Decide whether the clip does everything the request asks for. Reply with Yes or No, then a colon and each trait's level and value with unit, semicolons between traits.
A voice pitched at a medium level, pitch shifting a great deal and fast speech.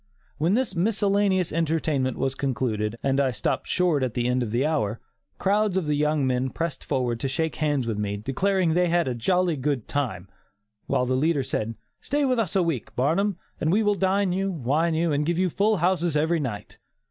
Yes: medium, 155 Hz; wide, 5.9 semitones; fast, 215 wpm